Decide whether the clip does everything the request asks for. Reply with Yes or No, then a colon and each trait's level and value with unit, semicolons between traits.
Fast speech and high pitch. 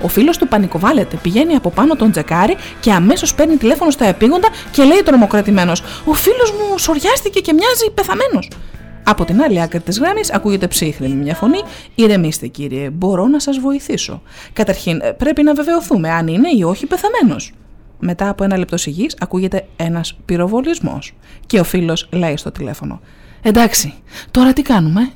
No: average, 160 wpm; high, 220 Hz